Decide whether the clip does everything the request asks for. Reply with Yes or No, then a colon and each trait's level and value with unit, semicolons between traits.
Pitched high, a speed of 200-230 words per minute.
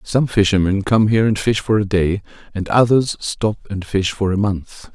No: low, 100 Hz; fast, 205 wpm